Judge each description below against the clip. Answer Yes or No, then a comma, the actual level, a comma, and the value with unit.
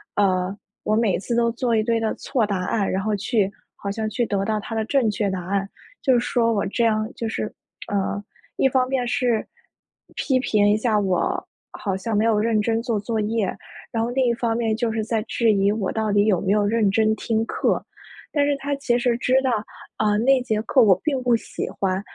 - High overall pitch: Yes, high, 220 Hz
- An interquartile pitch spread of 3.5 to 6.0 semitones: No, narrow, 2.5 semitones